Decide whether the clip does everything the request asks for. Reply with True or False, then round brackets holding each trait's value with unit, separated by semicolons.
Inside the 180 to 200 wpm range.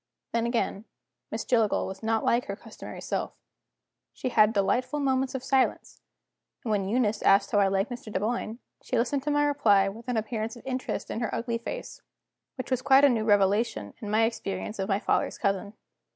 True (195 wpm)